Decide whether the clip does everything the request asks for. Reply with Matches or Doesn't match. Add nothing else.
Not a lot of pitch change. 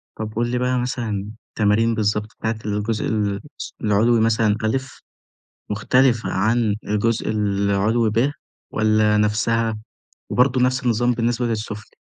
Matches